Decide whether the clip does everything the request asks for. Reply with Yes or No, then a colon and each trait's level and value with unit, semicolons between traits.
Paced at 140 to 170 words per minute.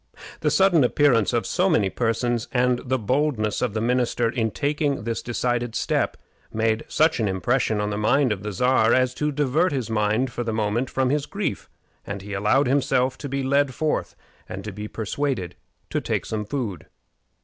No: average, 190 wpm